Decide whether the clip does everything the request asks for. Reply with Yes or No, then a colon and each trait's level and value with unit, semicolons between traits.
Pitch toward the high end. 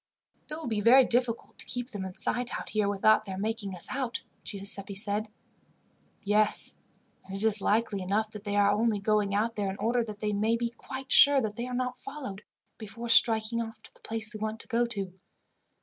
Yes: high, 215 Hz